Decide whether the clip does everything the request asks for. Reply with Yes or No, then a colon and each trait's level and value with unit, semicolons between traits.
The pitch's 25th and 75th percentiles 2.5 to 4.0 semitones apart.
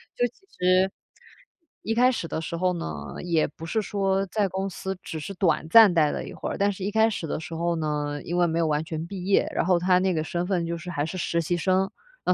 Yes: average, 2.8 semitones